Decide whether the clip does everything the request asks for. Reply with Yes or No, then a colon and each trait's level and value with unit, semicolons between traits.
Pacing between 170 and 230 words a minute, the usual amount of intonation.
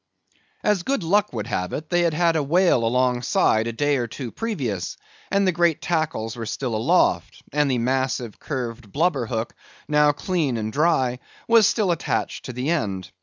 No: average, 180 wpm; wide, 6.6 semitones